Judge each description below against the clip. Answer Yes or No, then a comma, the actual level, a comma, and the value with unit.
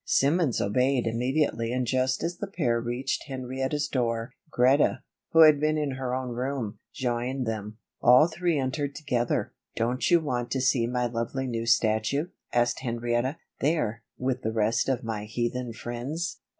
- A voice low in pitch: Yes, low, 125 Hz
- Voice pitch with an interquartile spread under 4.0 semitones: Yes, average, 2.9 semitones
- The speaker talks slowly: No, average, 160 wpm